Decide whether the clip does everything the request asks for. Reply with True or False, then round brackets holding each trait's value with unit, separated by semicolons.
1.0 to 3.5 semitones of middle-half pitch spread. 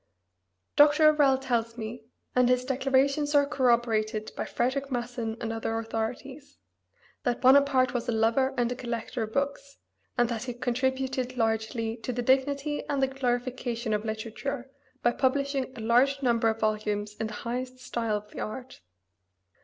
True (2.9 semitones)